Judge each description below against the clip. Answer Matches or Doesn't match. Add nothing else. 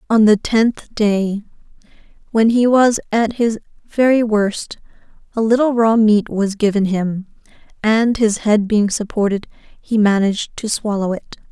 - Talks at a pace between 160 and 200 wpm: Doesn't match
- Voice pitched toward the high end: Matches